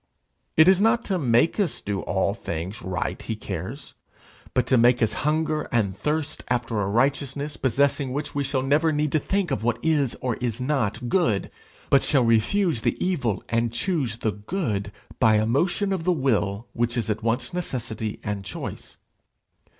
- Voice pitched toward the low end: Yes, low, 125 Hz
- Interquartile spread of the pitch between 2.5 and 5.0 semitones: No, wide, 5.5 semitones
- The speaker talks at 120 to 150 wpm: No, average, 180 wpm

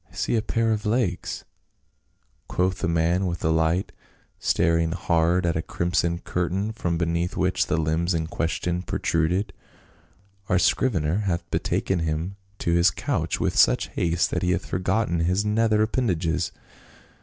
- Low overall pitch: Yes, very low, 90 Hz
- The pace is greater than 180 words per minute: No, average, 160 wpm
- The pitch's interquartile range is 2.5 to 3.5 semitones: Yes, average, 2.8 semitones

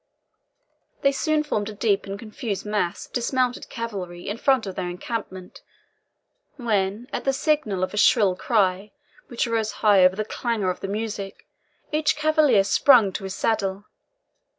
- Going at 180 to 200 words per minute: No, average, 160 wpm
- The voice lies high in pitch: Yes, high, 215 Hz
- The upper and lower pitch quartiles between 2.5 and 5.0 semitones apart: Yes, average, 4.0 semitones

